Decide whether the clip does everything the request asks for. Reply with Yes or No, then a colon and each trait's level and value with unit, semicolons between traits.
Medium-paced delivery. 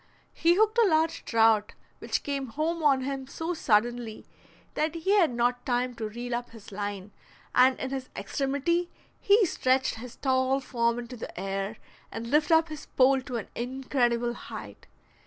Yes: average, 170 wpm